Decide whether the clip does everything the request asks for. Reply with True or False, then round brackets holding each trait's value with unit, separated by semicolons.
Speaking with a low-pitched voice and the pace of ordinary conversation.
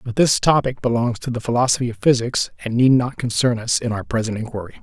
False (120 Hz; 225 wpm)